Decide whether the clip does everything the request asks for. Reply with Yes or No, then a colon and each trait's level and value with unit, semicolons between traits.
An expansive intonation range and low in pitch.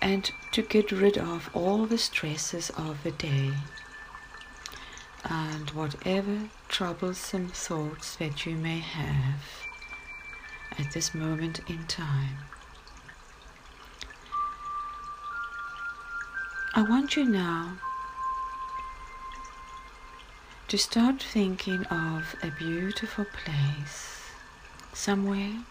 No: wide, 6.6 semitones; high, 195 Hz